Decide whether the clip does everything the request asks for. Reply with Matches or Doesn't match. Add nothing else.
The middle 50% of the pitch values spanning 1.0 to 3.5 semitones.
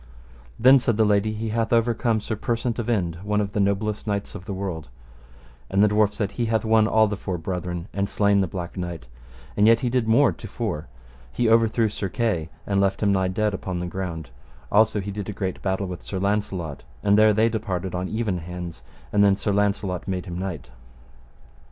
Matches